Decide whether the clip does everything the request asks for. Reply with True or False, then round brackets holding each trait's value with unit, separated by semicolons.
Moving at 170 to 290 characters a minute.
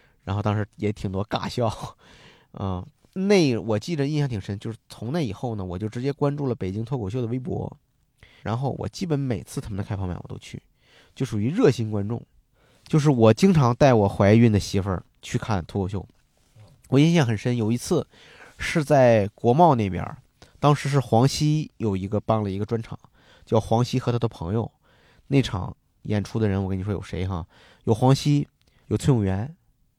True (275 characters per minute)